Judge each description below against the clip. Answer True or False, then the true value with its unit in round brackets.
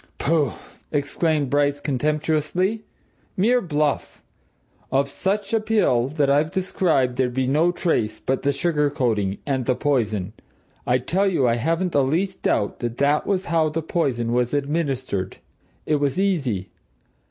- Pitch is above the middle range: False (145 Hz)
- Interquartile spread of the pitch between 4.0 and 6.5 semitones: True (4.6 semitones)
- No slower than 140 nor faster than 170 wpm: True (155 wpm)